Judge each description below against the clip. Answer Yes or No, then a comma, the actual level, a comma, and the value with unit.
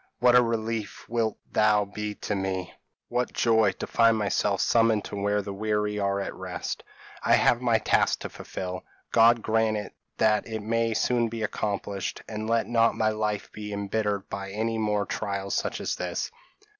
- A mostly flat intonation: Yes, narrow, 2.0 semitones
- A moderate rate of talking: Yes, average, 175 wpm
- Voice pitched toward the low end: Yes, low, 105 Hz